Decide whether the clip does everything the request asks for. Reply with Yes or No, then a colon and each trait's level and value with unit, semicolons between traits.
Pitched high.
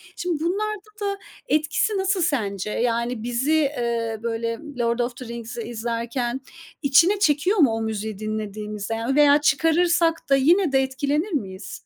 Yes: very high, 260 Hz